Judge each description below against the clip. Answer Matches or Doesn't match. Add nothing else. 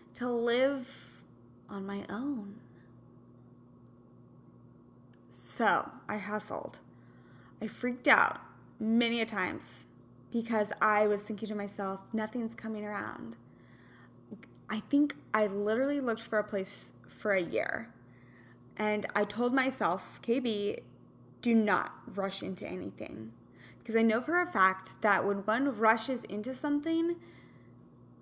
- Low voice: Doesn't match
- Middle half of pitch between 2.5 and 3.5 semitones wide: Matches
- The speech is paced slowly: Matches